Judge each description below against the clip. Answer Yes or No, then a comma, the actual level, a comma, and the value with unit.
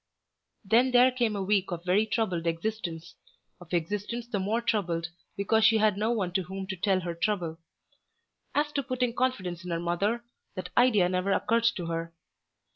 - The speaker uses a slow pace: No, average, 180 wpm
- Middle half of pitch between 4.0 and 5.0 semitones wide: Yes, average, 4.5 semitones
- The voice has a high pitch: Yes, high, 195 Hz